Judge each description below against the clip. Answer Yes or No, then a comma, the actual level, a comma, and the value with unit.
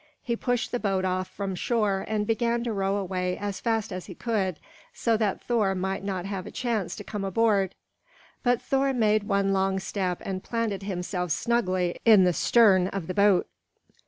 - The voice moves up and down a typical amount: Yes, average, 3.2 semitones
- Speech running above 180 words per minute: Yes, average, 190 wpm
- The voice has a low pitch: No, high, 200 Hz